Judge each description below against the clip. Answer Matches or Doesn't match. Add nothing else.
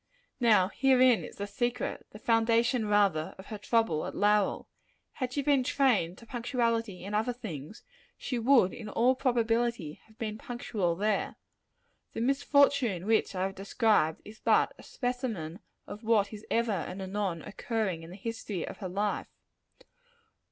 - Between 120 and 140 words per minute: Doesn't match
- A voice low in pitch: Doesn't match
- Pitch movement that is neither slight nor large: Matches